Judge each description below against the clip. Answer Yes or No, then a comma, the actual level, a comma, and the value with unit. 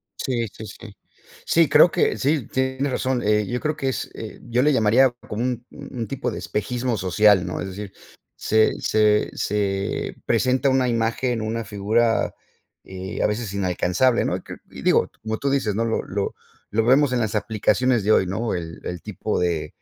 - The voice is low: Yes, low, 110 Hz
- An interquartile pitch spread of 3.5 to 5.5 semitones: Yes, average, 3.8 semitones